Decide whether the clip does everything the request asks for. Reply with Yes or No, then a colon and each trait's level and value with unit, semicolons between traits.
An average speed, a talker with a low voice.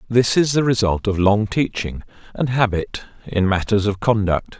Yes: average, 170 wpm; low, 105 Hz